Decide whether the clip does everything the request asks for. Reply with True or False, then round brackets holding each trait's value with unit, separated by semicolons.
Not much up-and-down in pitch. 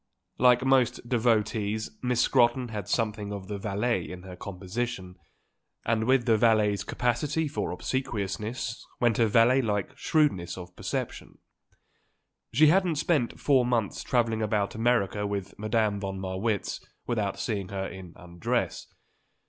False (3.4 semitones)